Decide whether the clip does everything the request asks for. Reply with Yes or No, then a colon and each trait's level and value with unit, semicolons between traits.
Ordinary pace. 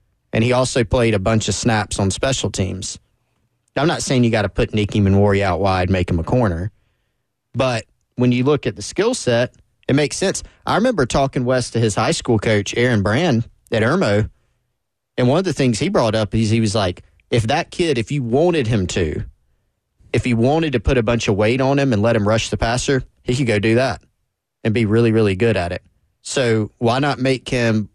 No: fast, 225 wpm